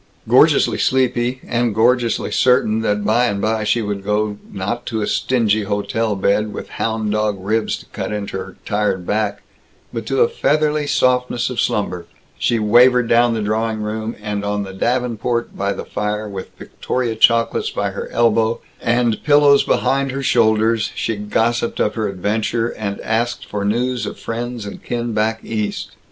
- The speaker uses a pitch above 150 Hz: No, low, 110 Hz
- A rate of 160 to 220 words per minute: Yes, average, 170 wpm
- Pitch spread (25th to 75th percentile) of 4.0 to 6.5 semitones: No, narrow, 2.4 semitones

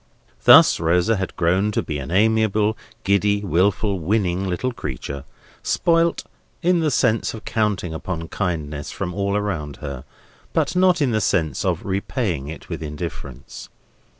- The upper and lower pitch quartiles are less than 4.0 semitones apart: No, average, 5.1 semitones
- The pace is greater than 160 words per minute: No, average, 150 wpm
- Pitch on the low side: Yes, very low, 95 Hz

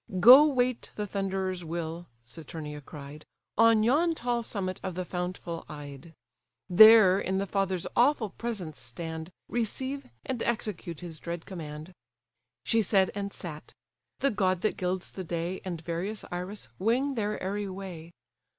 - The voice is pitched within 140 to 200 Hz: Yes, medium, 185 Hz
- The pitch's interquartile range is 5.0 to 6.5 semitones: No, average, 4.5 semitones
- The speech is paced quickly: No, average, 145 wpm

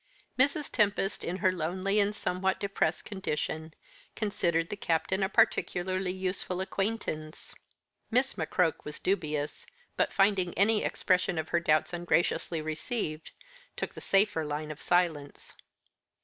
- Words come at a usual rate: No, slow, 130 wpm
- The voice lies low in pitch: No, medium, 185 Hz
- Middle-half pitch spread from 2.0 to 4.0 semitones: Yes, average, 3.7 semitones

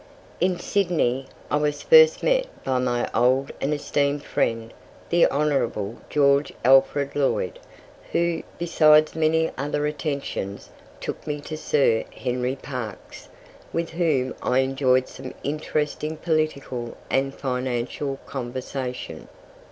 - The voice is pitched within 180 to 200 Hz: No, medium, 140 Hz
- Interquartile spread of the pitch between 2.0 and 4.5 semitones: Yes, average, 3.2 semitones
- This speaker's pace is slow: Yes, slow, 115 wpm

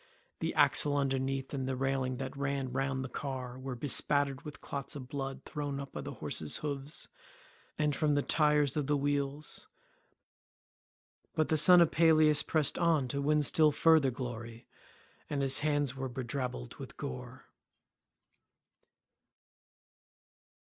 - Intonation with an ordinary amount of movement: No, narrow, 2.1 semitones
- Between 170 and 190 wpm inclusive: No, average, 140 wpm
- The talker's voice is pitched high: No, medium, 140 Hz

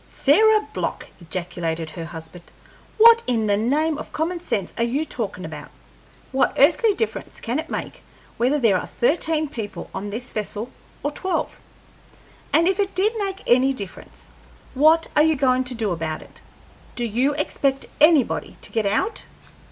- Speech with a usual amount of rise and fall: No, wide, 7.2 semitones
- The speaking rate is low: No, average, 165 wpm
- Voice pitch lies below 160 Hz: No, very high, 265 Hz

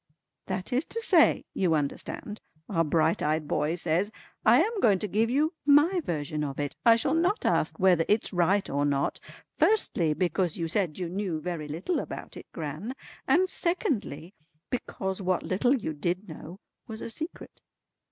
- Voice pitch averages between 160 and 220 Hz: Yes, medium, 185 Hz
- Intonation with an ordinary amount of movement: No, wide, 7.0 semitones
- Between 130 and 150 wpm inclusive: No, average, 170 wpm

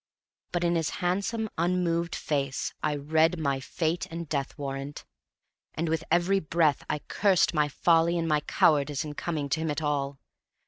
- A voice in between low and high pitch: Yes, medium, 160 Hz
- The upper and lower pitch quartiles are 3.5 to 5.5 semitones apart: No, average, 2.7 semitones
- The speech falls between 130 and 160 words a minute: No, average, 170 wpm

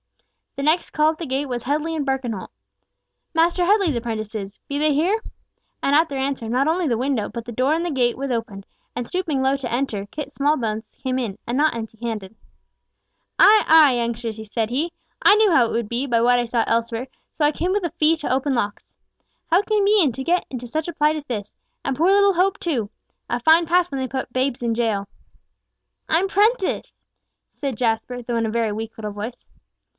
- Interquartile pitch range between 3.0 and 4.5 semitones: No, wide, 5.5 semitones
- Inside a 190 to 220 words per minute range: Yes, fast, 205 wpm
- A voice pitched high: Yes, very high, 265 Hz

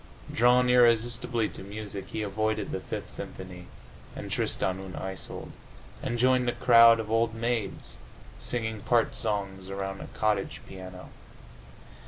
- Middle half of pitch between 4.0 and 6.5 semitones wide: No, average, 3.4 semitones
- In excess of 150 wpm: No, slow, 135 wpm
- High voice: No, low, 110 Hz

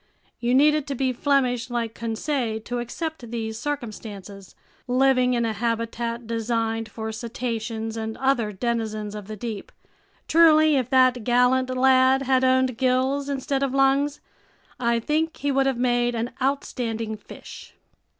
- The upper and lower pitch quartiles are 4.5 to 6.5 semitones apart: No, average, 3.0 semitones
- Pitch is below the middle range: No, high, 245 Hz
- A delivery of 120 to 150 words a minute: Yes, average, 145 wpm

